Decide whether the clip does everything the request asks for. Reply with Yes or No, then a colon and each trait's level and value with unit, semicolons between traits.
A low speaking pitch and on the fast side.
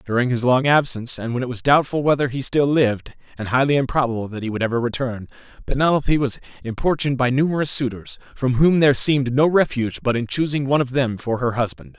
Yes: low, 130 Hz; fast, 210 wpm